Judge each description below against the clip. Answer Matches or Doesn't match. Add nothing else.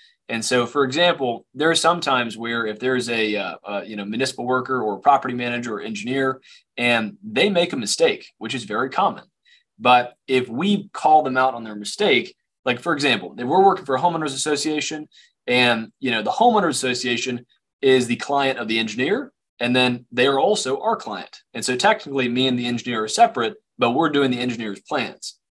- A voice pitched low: Matches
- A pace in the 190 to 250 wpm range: Matches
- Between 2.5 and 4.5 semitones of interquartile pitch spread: Matches